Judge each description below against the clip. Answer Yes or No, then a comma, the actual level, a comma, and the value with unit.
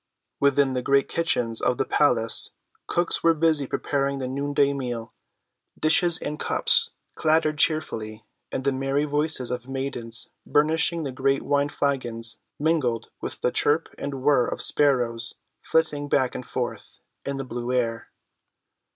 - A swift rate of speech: No, average, 140 wpm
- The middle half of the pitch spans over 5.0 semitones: No, average, 3.3 semitones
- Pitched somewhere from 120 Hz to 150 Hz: Yes, medium, 140 Hz